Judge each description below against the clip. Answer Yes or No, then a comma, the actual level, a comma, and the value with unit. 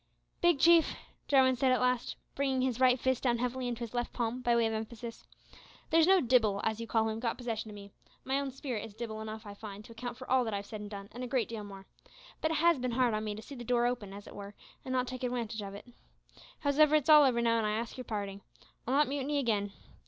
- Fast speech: Yes, fast, 265 wpm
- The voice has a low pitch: No, high, 240 Hz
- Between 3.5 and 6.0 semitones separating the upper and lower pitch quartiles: No, average, 3.1 semitones